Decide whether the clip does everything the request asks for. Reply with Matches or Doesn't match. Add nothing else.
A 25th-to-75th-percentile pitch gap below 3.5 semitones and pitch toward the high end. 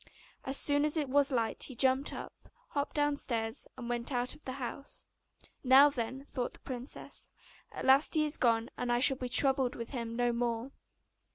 Matches